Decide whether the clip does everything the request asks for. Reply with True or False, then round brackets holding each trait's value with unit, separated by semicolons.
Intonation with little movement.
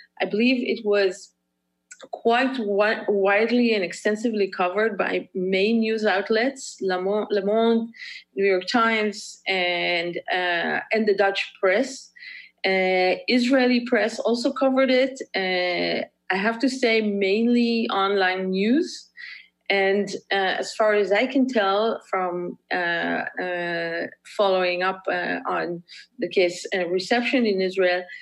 False (3.7 semitones)